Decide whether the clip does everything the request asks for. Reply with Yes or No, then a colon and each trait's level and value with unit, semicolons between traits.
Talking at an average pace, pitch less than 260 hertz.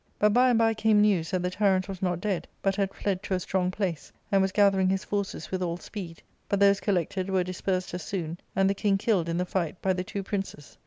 No: fast, 255 wpm; high, 190 Hz